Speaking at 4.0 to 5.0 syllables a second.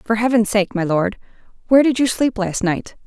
No: 5.4 syllables/s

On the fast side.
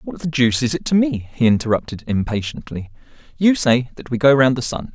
Yes: fast, 220 wpm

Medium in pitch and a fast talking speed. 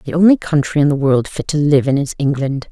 Yes: medium, 145 Hz; fast, 265 wpm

